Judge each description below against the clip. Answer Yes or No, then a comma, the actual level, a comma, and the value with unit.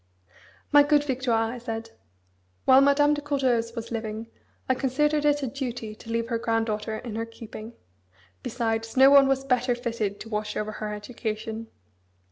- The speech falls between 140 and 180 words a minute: Yes, average, 165 wpm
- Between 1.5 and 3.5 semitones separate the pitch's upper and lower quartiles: Yes, average, 3.2 semitones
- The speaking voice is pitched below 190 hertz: No, high, 235 Hz